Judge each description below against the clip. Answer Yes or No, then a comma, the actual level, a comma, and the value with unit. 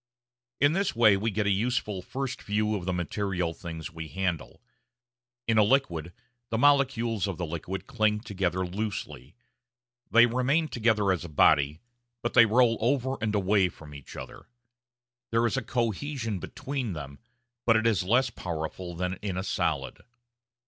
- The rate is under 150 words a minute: No, average, 160 wpm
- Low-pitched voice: Yes, low, 105 Hz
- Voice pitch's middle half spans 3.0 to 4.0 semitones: No, average, 4.6 semitones